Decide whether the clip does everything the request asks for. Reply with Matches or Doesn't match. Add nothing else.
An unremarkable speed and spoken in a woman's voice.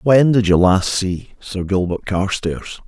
Doesn't match